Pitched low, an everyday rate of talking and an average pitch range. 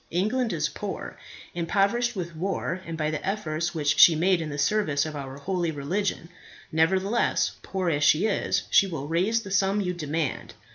No: medium, 175 Hz; average, 180 wpm; average, 4.1 semitones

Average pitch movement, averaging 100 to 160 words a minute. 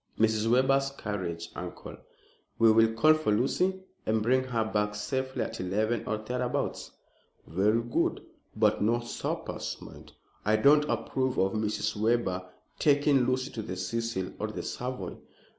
Yes: average, 3.5 semitones; average, 145 wpm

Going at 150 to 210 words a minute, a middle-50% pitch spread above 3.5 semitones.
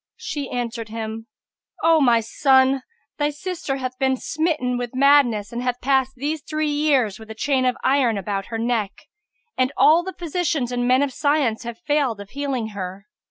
Yes: average, 180 wpm; average, 4.0 semitones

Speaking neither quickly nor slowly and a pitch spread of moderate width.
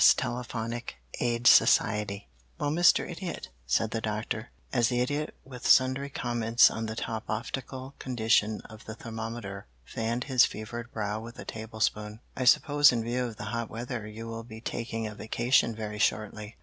No: average, 165 wpm; narrow, 2.1 semitones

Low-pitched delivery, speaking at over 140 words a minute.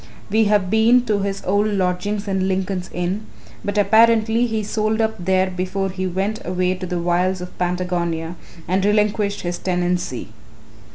No: high, 190 Hz; average, 160 wpm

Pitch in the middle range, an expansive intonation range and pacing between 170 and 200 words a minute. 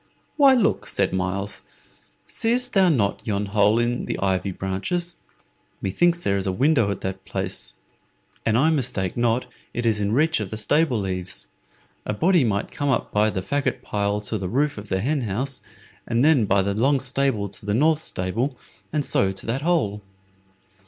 No: low, 115 Hz; wide, 6.3 semitones; average, 185 wpm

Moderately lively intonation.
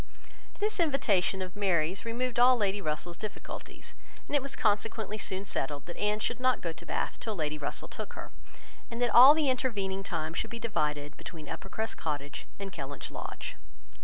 No: wide, 6.2 semitones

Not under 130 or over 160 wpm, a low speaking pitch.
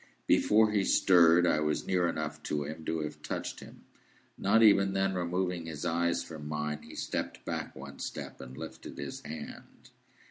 No: average, 175 wpm; very low, 85 Hz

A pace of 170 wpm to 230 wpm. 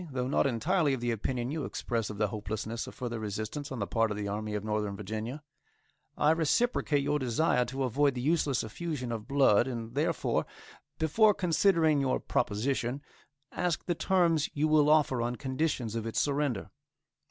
Yes: average, 175 wpm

